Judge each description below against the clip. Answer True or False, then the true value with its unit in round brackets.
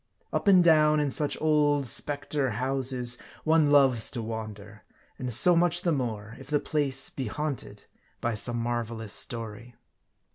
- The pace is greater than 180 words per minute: False (150 wpm)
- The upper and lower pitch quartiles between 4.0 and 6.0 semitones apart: True (4.4 semitones)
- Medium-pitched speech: False (130 Hz)